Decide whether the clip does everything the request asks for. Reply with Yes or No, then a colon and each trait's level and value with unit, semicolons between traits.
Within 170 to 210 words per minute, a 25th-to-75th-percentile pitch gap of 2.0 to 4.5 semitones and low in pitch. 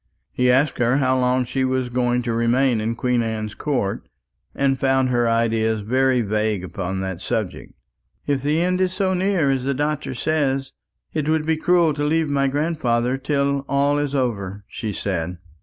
Yes: average, 180 wpm; average, 4.0 semitones; low, 130 Hz